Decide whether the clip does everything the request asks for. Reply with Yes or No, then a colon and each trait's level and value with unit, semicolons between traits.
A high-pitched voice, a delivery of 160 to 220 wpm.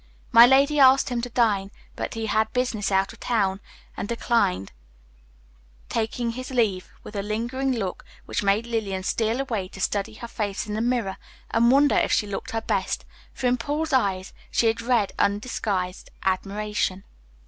Yes: high, 225 Hz; average, 170 wpm